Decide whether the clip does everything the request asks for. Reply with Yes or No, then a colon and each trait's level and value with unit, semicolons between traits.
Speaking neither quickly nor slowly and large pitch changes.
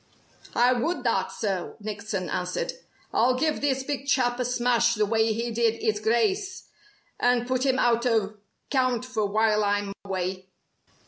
No: average, 155 wpm; average, 3.2 semitones